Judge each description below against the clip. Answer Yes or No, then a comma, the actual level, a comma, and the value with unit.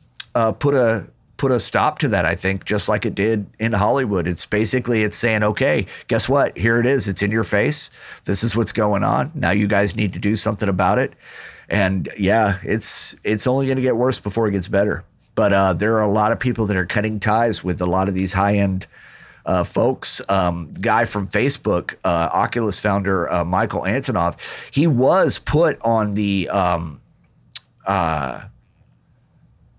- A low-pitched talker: Yes, low, 105 Hz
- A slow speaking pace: No, average, 190 wpm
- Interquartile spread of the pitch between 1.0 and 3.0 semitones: Yes, average, 2.7 semitones